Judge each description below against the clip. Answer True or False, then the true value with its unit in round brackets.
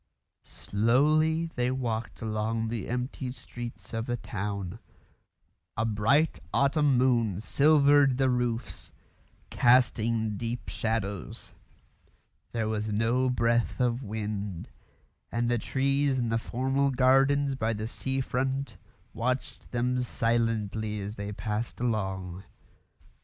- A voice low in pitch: True (120 Hz)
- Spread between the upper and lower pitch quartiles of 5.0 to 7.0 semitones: False (3.2 semitones)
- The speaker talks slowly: True (115 wpm)